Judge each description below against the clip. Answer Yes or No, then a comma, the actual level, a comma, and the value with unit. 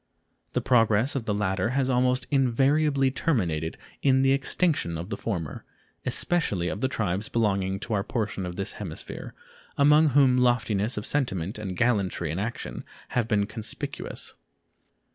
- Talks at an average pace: Yes, average, 150 wpm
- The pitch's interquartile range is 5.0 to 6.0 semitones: Yes, average, 5.3 semitones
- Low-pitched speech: Yes, low, 115 Hz